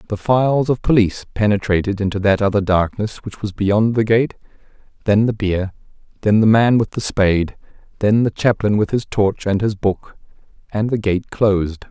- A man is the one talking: Yes, male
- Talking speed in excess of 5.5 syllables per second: No, 5.1 syllables/s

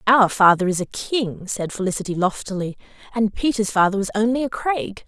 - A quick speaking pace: No, average, 175 wpm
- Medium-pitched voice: No, high, 210 Hz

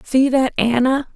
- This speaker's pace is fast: No, average, 155 wpm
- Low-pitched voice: No, very high, 260 Hz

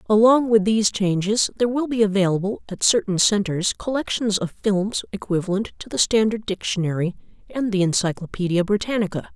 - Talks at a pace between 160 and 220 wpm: No, average, 150 wpm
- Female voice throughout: Yes, female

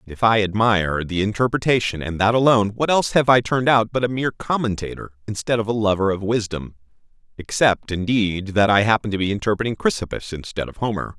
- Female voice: No, male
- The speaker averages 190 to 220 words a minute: Yes, average, 195 wpm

